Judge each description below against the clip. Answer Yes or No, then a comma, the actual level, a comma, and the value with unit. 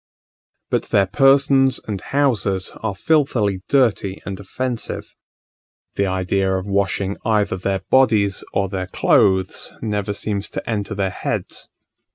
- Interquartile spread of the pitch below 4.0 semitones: Yes, average, 3.3 semitones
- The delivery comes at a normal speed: No, slow, 130 wpm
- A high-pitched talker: No, low, 100 Hz